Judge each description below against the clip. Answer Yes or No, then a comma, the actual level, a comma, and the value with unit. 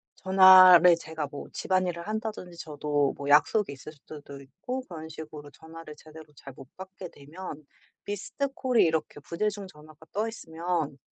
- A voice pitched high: No, medium, 165 Hz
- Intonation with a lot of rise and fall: No, average, 3.9 semitones